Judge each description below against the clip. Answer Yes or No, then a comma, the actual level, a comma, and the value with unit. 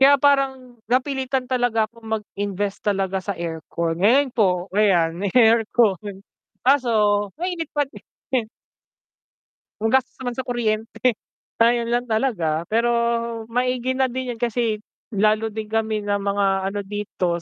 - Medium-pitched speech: No, high, 225 Hz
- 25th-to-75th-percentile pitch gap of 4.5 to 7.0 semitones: No, average, 3.8 semitones